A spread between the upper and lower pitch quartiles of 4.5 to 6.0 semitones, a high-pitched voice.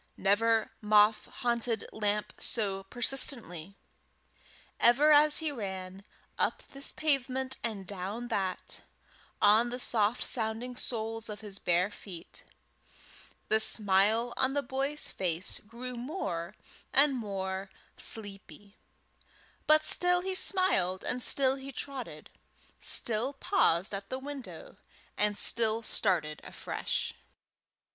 Yes: average, 4.9 semitones; high, 225 Hz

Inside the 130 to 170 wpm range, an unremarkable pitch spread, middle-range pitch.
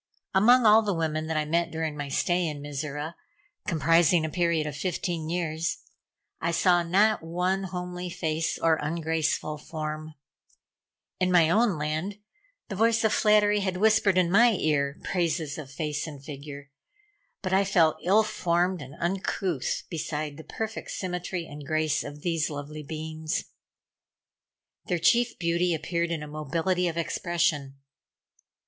Yes: average, 150 wpm; average, 3.0 semitones; medium, 165 Hz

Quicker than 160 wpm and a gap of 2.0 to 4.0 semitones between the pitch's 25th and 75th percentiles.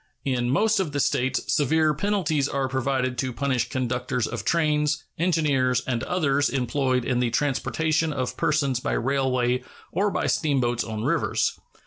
No: average, 150 wpm; average, 3.2 semitones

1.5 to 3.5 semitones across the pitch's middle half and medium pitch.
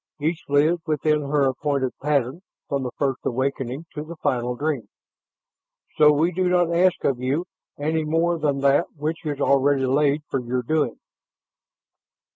Yes: average, 2.8 semitones; medium, 145 Hz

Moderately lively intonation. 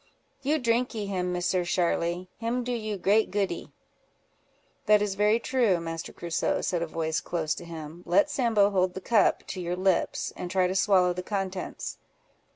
Yes: average, 3.2 semitones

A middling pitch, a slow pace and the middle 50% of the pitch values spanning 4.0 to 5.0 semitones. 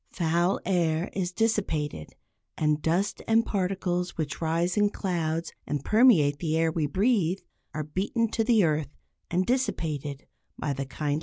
No: medium, 170 Hz; average, 155 wpm; average, 4.4 semitones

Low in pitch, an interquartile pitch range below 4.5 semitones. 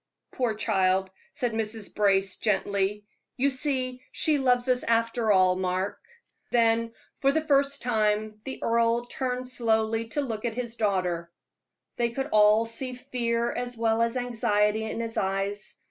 No: high, 230 Hz; average, 2.9 semitones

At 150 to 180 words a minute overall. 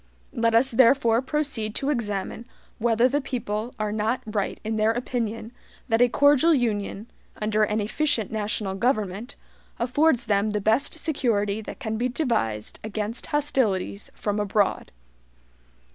No: average, 140 wpm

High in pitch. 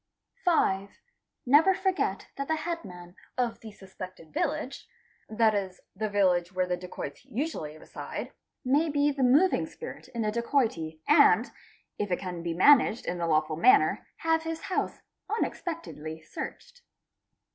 Yes: high, 225 Hz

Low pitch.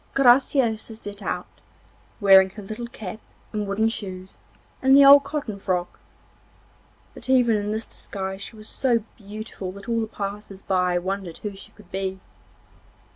No: high, 210 Hz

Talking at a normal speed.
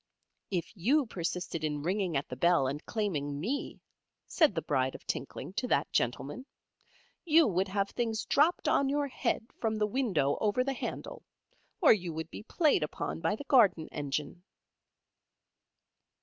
Yes: average, 160 wpm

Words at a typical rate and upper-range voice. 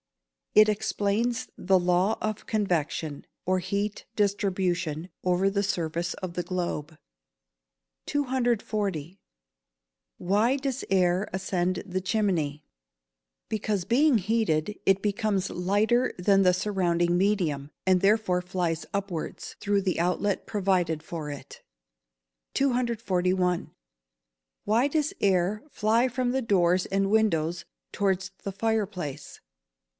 No: slow, 115 wpm; high, 195 Hz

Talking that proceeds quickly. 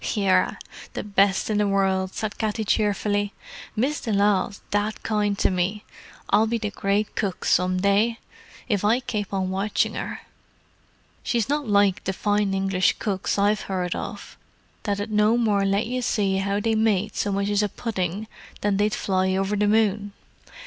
No: average, 170 wpm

